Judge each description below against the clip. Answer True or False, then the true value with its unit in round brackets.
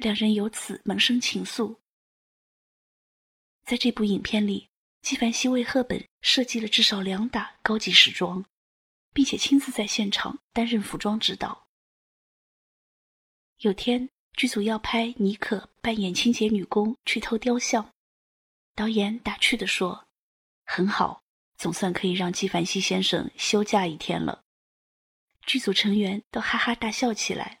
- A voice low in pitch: False (215 Hz)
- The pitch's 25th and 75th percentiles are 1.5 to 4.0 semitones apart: True (3.0 semitones)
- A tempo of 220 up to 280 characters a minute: False (210 characters per minute)